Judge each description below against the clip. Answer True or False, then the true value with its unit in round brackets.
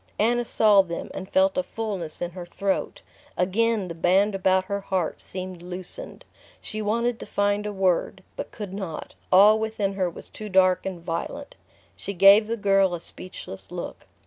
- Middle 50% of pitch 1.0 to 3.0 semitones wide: True (2.7 semitones)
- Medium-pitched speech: False (195 Hz)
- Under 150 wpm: False (175 wpm)